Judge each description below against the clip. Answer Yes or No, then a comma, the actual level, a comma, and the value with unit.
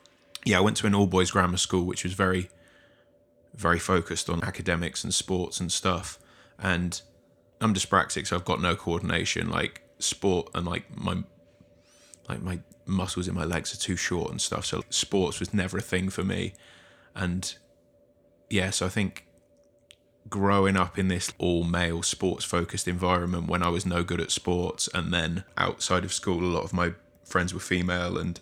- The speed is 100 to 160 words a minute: No, average, 175 wpm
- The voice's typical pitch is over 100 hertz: No, very low, 90 Hz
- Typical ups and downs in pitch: No, narrow, 2.2 semitones